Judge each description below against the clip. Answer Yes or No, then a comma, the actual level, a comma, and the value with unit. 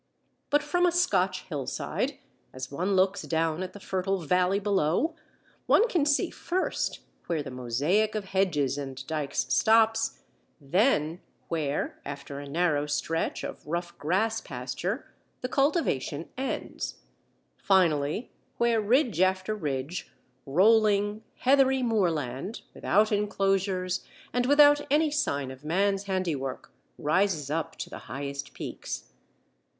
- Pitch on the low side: No, medium, 185 Hz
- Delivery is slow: Yes, slow, 125 wpm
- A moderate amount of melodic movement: No, wide, 6.7 semitones